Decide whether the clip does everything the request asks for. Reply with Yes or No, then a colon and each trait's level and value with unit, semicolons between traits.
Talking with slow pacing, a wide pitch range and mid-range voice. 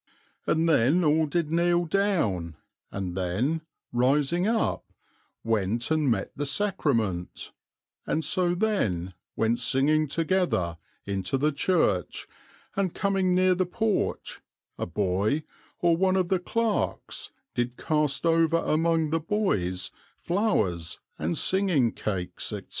Yes: slow, 125 wpm; wide, 8.6 semitones; medium, 155 Hz